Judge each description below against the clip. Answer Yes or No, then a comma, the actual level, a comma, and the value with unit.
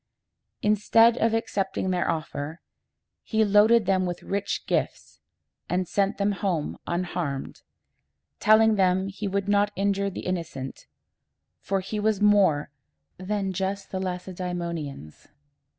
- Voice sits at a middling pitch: No, high, 195 Hz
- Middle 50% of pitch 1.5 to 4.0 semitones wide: Yes, narrow, 2.6 semitones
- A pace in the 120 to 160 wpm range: Yes, slow, 135 wpm